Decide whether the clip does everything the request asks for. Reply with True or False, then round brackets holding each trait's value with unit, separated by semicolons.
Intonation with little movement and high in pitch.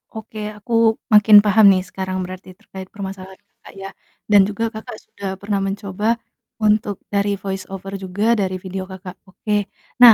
True (1.8 semitones; 195 Hz)